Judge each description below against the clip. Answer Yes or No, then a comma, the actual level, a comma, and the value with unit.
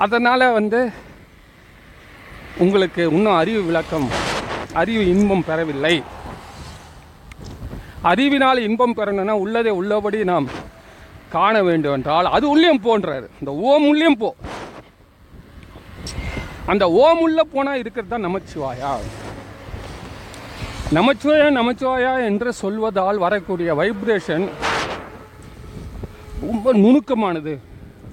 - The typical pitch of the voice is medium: No, high, 200 Hz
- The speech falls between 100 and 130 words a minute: No, average, 85 wpm